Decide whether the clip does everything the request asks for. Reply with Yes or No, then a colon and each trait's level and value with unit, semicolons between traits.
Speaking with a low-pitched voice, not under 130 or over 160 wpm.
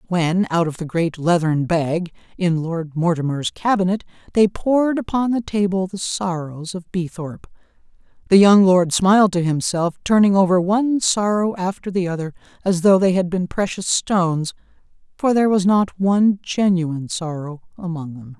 No: medium, 180 Hz; average, 155 wpm